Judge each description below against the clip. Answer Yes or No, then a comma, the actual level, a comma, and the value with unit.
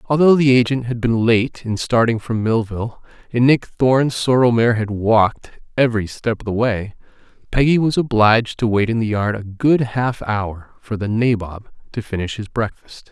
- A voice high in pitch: No, low, 115 Hz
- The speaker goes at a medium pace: Yes, average, 190 wpm